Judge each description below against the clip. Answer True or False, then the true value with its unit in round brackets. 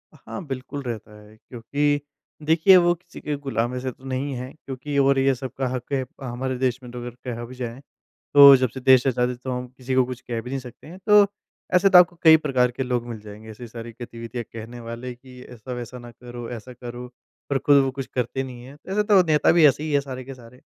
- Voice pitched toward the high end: False (130 Hz)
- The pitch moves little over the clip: True (2.3 semitones)